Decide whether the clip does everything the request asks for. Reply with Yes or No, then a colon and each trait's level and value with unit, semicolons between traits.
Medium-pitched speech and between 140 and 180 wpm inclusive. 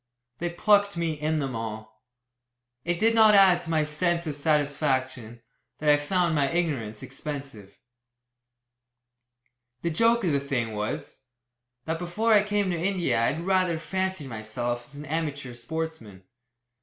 Yes: medium, 155 Hz; average, 150 wpm